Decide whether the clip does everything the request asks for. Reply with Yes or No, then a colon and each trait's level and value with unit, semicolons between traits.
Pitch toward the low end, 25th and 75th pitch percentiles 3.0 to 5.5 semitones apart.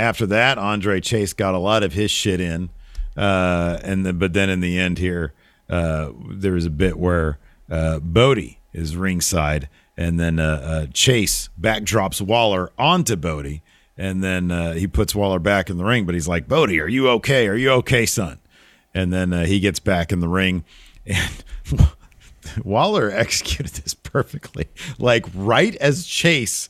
Yes: very low, 90 Hz; average, 3.9 semitones